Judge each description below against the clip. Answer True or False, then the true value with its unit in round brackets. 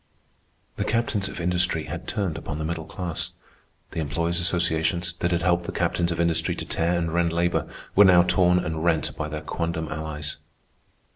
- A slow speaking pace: False (185 wpm)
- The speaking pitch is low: True (85 Hz)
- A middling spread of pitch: False (1.7 semitones)